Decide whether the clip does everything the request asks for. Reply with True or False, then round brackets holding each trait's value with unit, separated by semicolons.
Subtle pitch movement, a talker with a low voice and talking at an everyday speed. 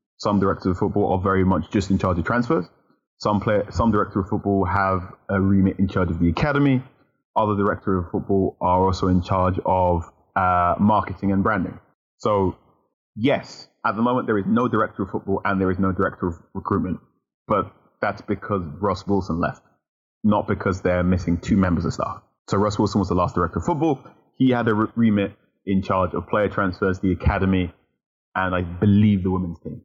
True (2.1 semitones; 95 Hz; 195 wpm)